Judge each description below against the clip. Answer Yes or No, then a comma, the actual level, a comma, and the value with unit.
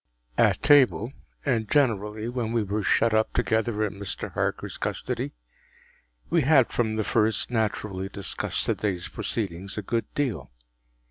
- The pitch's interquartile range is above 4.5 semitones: No, average, 2.8 semitones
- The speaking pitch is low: Yes, low, 110 Hz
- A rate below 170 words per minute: Yes, average, 145 wpm